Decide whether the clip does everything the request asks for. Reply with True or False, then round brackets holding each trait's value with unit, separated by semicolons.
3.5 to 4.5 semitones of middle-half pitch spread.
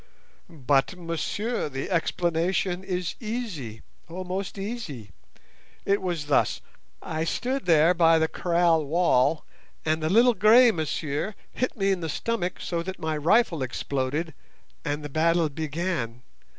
True (3.8 semitones)